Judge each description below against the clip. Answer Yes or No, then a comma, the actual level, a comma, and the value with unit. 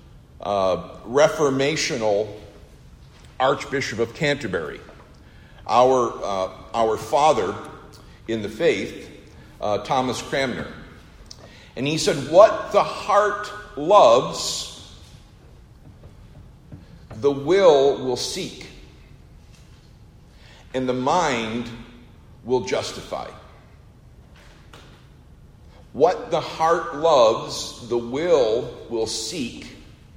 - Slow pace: Yes, slow, 75 wpm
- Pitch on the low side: Yes, low, 120 Hz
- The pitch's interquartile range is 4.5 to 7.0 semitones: Yes, average, 5.2 semitones